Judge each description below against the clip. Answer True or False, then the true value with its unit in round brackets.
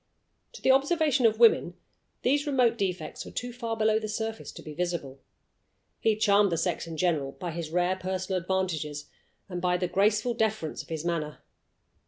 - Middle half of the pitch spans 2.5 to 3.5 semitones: False (4.7 semitones)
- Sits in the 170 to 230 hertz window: True (190 Hz)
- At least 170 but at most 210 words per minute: True (180 wpm)